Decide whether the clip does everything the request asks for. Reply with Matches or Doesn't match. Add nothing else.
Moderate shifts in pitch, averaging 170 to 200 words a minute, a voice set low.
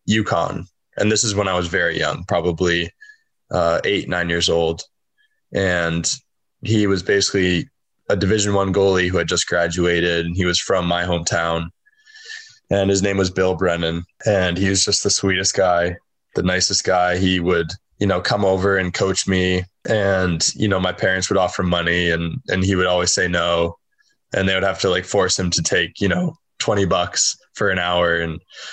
Doesn't match